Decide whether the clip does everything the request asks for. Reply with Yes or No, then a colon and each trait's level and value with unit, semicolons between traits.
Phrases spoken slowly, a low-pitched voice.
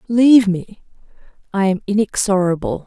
No: slow, 105 wpm; high, 205 Hz